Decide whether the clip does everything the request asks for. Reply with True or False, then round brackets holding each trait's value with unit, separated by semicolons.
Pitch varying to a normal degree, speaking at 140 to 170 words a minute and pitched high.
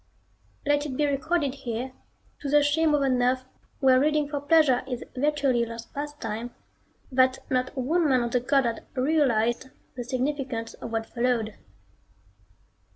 True (3.0 semitones; 155 wpm; 260 Hz)